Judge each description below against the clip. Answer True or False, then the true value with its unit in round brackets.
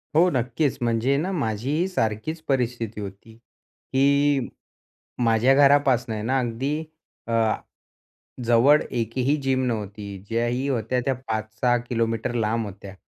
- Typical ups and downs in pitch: True (3.3 semitones)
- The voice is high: False (120 Hz)